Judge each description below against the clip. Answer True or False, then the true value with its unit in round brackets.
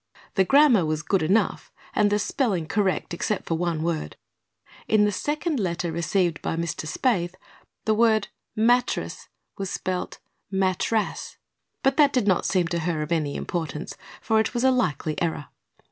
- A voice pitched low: False (185 Hz)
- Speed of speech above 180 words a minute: False (160 wpm)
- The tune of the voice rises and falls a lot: False (4.8 semitones)